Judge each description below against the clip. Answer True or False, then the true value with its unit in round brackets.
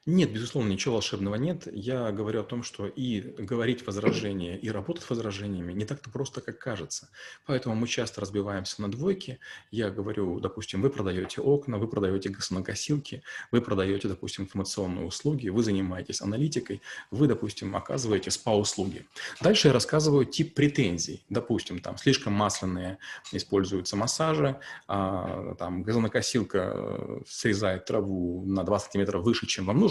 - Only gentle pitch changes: False (4.5 semitones)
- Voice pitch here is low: True (105 Hz)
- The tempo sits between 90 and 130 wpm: False (140 wpm)